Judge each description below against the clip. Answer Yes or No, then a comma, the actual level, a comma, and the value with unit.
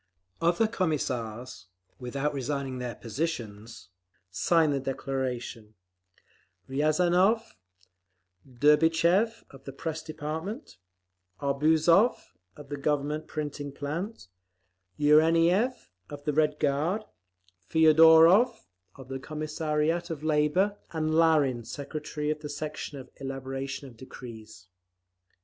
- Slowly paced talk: Yes, slow, 95 wpm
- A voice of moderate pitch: Yes, medium, 150 Hz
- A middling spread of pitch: Yes, average, 3.4 semitones